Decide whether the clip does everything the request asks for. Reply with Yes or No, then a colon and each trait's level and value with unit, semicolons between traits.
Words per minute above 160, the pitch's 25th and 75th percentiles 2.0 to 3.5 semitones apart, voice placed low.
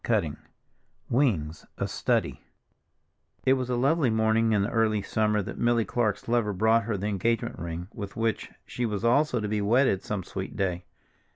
Yes: average, 180 wpm; average, 2.9 semitones; low, 110 Hz